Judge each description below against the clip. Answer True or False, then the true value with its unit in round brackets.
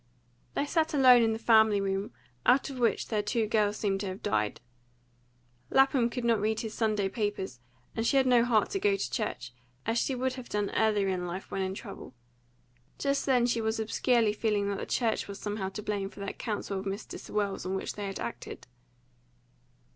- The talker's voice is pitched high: True (210 Hz)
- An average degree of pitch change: True (3.1 semitones)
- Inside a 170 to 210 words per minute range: True (205 wpm)